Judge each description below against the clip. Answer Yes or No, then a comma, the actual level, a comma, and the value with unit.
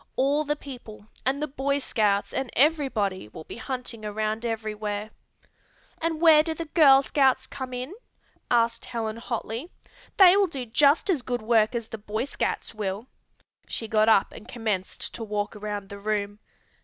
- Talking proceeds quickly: No, average, 170 wpm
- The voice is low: No, high, 235 Hz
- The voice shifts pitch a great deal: No, average, 4.5 semitones